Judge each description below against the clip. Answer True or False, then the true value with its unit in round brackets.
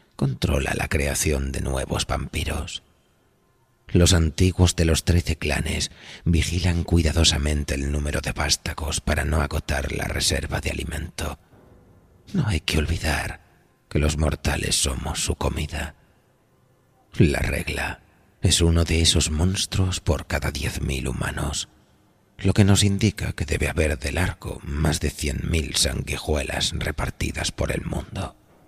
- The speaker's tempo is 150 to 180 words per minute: False (135 wpm)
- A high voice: False (85 Hz)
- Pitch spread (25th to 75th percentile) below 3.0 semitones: False (3.6 semitones)